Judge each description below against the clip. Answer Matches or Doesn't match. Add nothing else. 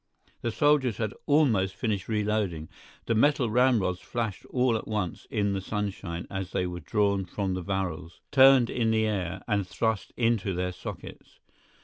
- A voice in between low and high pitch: Doesn't match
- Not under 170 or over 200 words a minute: Doesn't match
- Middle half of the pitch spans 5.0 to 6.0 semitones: Doesn't match